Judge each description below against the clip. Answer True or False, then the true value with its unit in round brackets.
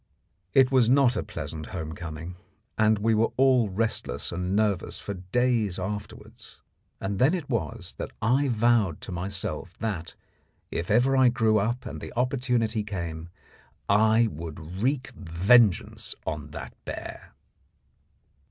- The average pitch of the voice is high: False (105 Hz)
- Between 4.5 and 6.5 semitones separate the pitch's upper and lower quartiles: True (5.2 semitones)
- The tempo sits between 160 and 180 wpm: False (140 wpm)